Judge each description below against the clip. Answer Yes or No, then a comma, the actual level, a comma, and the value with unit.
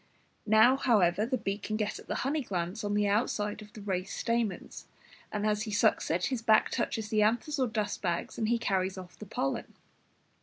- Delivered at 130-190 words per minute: No, fast, 205 wpm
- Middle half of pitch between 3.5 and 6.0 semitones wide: No, narrow, 2.5 semitones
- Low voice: No, high, 210 Hz